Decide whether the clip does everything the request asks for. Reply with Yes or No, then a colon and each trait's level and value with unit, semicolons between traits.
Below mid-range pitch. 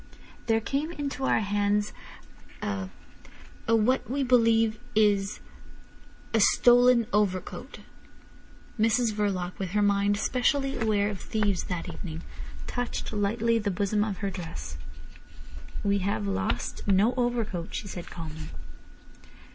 No: high, 210 Hz